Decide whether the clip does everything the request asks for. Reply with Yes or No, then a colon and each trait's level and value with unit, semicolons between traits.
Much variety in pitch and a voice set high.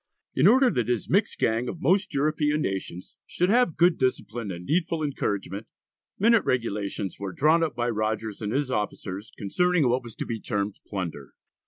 No: wide, 7.5 semitones; low, 120 Hz